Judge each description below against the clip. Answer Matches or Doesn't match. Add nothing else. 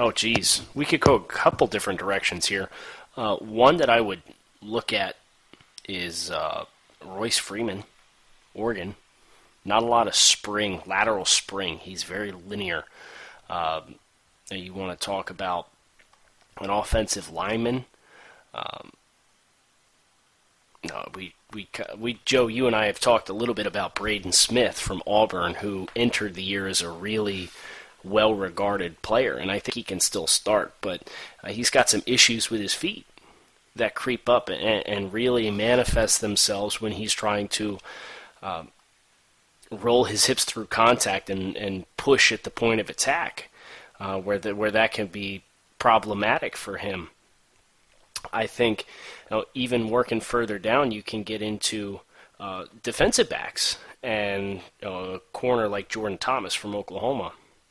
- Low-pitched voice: Matches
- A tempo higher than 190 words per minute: Doesn't match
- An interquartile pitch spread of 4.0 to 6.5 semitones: Doesn't match